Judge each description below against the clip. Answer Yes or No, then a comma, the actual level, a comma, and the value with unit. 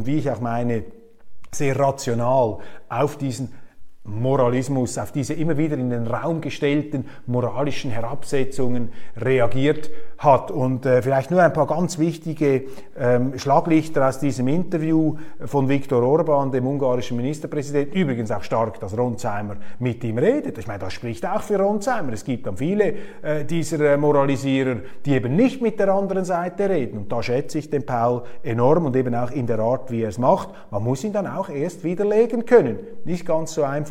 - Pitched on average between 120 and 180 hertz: Yes, medium, 140 Hz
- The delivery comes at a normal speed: Yes, average, 180 wpm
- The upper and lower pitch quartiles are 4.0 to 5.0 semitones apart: Yes, average, 4.5 semitones